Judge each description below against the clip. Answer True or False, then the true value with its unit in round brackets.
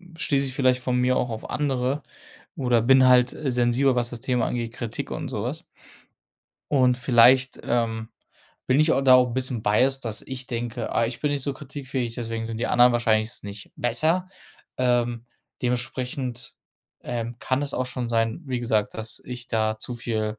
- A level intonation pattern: True (1.9 semitones)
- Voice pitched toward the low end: True (125 Hz)